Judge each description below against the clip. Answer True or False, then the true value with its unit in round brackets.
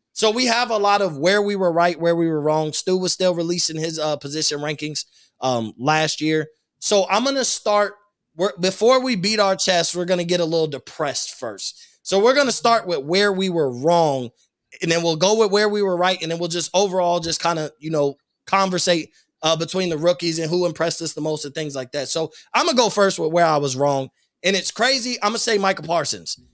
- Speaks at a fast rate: True (245 wpm)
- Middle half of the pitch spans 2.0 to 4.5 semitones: True (4.0 semitones)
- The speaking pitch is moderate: True (175 Hz)